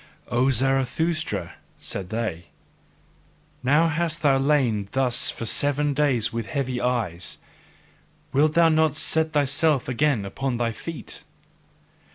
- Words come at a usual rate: No, slow, 120 wpm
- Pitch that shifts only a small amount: No, average, 4.2 semitones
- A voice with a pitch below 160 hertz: Yes, low, 135 Hz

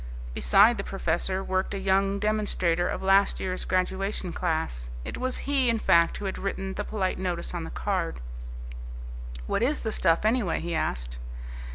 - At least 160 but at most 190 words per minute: Yes, average, 170 wpm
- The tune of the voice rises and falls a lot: No, average, 3.1 semitones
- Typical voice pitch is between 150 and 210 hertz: Yes, high, 190 Hz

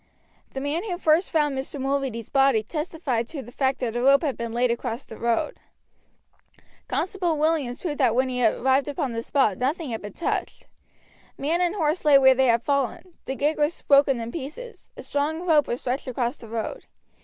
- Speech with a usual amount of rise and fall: Yes, average, 4.0 semitones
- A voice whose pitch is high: Yes, very high, 275 Hz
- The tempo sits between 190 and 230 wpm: Yes, average, 200 wpm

